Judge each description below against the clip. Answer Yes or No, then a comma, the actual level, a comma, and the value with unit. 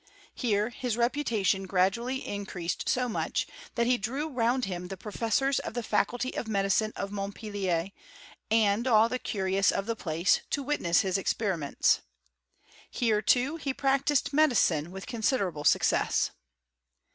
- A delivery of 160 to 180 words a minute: No, average, 140 wpm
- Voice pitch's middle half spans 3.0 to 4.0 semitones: No, average, 4.4 semitones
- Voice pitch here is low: No, high, 220 Hz